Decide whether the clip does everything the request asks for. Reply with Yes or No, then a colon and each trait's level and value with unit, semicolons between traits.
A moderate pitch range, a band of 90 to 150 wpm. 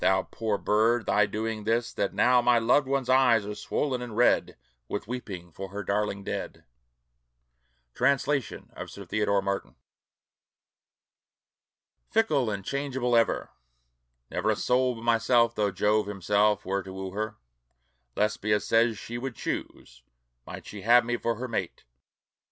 Yes: average, 3.2 semitones; average, 145 wpm